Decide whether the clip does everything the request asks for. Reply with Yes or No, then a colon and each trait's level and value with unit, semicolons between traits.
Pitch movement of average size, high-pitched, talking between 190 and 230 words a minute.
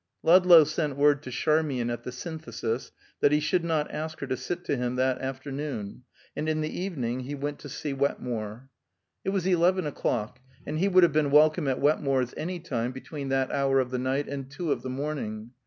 No: average, 3.3 semitones; medium, 140 Hz; fast, 205 wpm